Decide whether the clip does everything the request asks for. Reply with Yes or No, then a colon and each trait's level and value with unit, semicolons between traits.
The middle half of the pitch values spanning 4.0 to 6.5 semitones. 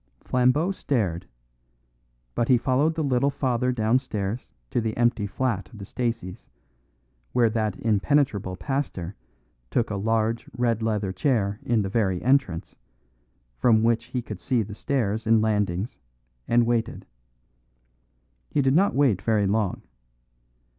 No: average, 3.6 semitones